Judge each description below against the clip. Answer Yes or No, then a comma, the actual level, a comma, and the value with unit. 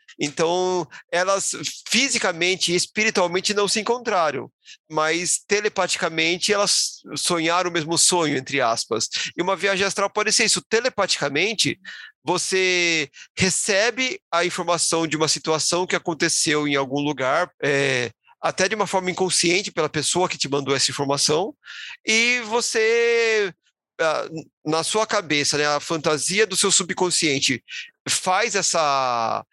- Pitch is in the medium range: Yes, medium, 180 Hz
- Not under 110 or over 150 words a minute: Yes, average, 130 wpm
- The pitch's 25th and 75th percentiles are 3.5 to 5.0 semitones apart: Yes, average, 4.4 semitones